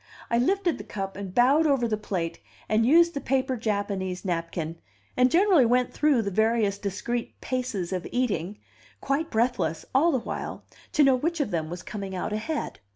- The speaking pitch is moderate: No, high, 230 Hz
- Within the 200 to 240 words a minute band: No, average, 180 wpm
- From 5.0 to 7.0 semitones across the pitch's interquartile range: Yes, wide, 5.6 semitones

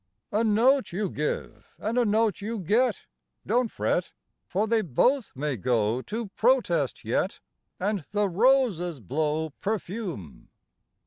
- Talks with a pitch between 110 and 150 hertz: No, high, 205 Hz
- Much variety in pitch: Yes, wide, 6.4 semitones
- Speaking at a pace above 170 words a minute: No, slow, 135 wpm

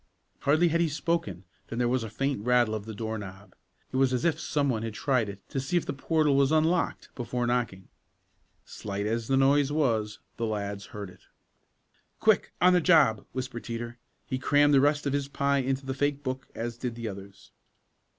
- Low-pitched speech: Yes, low, 130 Hz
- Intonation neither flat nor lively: Yes, average, 4.3 semitones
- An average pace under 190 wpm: No, fast, 205 wpm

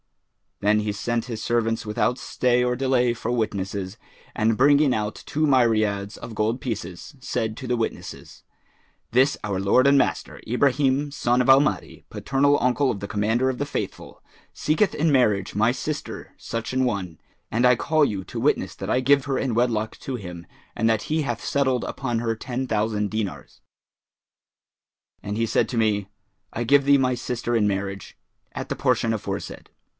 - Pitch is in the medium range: No, low, 120 Hz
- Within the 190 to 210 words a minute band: No, average, 180 wpm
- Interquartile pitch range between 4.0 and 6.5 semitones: No, average, 3.6 semitones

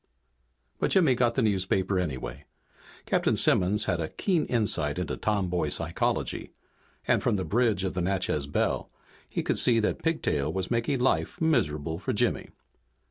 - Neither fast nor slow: Yes, average, 155 wpm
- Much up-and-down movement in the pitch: Yes, wide, 5.8 semitones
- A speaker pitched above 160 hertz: No, very low, 95 Hz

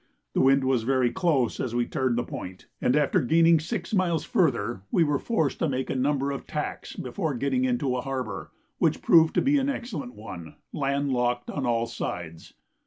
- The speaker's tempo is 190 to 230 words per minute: Yes, average, 195 wpm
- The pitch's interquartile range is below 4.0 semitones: No, average, 4.7 semitones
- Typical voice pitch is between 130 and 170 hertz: Yes, low, 135 Hz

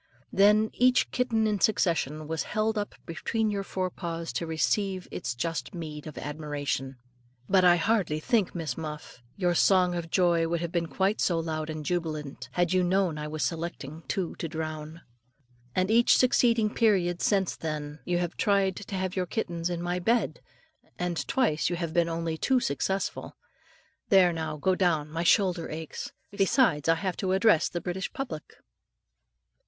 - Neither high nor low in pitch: Yes, medium, 175 Hz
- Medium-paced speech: Yes, average, 170 wpm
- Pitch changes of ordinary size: Yes, average, 3.5 semitones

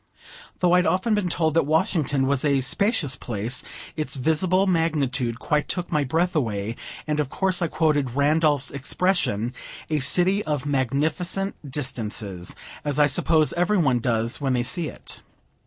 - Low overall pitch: No, medium, 150 Hz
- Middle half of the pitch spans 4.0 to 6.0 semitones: Yes, average, 4.9 semitones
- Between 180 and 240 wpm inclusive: No, average, 155 wpm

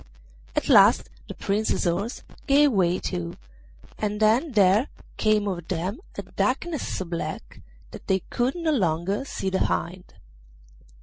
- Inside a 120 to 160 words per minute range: Yes, average, 140 wpm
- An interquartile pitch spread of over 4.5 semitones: Yes, average, 5.0 semitones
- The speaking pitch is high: Yes, high, 200 Hz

